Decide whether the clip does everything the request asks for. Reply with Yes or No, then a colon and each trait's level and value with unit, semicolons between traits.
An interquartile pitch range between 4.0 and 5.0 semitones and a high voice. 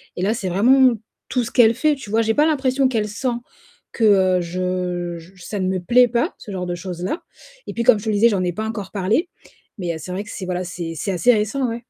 Yes: average, 4.7 semitones; high, 205 Hz